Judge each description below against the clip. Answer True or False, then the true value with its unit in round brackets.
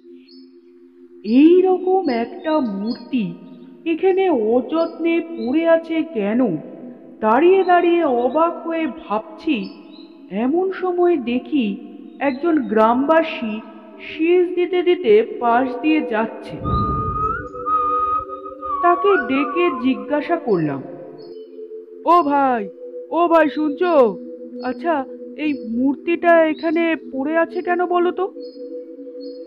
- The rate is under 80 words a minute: False (85 wpm)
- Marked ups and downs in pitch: True (6.0 semitones)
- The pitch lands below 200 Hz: False (315 Hz)